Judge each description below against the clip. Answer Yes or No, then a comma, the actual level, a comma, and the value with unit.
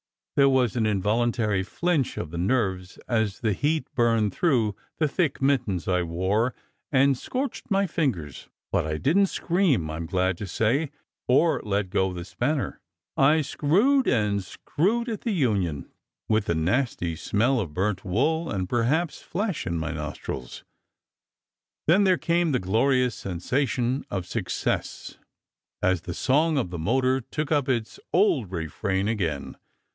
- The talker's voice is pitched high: No, low, 115 Hz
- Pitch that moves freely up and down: Yes, wide, 7.7 semitones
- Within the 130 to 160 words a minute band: Yes, average, 155 wpm